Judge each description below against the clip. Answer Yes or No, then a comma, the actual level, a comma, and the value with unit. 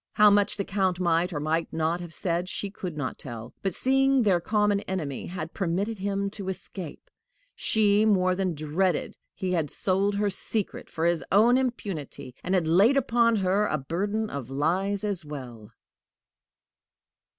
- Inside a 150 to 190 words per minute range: Yes, average, 165 wpm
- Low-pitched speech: No, medium, 185 Hz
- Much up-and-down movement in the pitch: No, average, 3.9 semitones